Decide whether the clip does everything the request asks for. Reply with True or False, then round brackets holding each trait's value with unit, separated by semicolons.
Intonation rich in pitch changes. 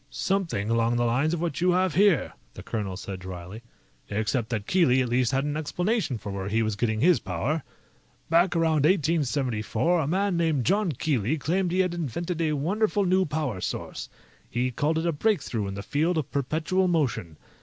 True (7.1 semitones)